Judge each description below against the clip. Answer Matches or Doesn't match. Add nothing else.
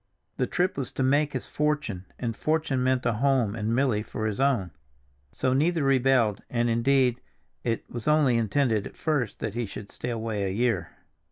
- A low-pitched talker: Matches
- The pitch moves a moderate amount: Matches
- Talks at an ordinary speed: Matches